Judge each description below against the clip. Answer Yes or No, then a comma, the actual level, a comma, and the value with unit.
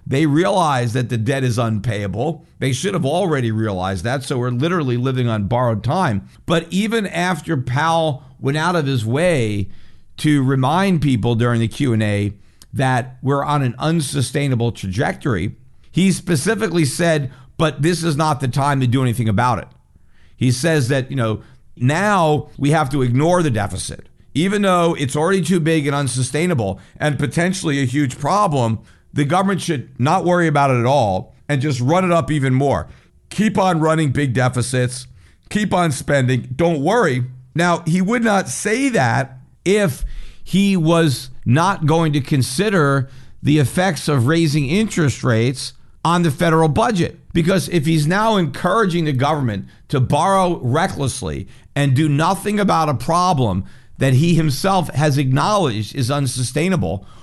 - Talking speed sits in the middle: Yes, average, 160 wpm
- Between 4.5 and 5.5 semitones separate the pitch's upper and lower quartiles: Yes, average, 5.2 semitones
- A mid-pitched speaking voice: Yes, medium, 145 Hz